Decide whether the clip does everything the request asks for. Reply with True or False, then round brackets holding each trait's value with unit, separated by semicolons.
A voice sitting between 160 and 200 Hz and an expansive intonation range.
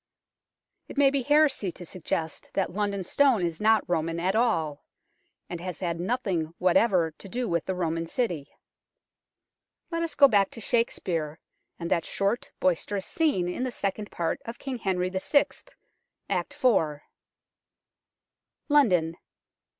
True (190 Hz; 5.9 semitones)